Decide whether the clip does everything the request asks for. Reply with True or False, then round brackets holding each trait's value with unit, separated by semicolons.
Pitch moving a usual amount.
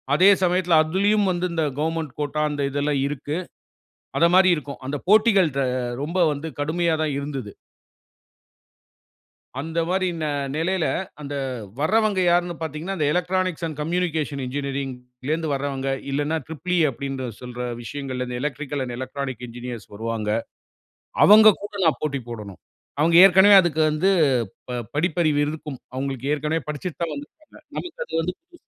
True (4.2 semitones)